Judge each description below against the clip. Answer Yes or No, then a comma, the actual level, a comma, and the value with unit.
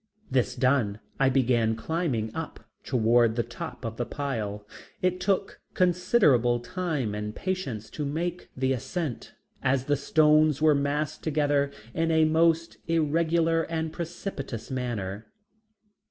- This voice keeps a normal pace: No, slow, 130 wpm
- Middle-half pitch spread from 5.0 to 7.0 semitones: Yes, average, 5.3 semitones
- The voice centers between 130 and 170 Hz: Yes, medium, 140 Hz